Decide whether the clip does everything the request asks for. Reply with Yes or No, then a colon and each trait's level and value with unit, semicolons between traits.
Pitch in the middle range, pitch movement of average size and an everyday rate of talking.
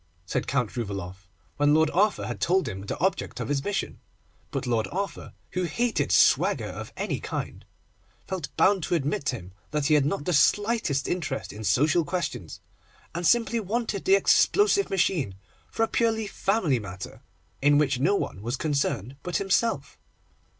No: medium, 155 Hz; wide, 7.1 semitones; average, 170 wpm